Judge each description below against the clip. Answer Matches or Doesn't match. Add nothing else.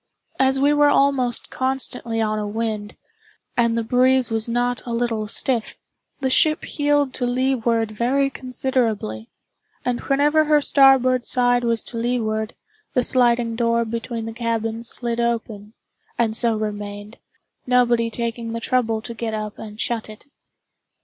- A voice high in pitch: Matches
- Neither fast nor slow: Matches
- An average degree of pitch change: Doesn't match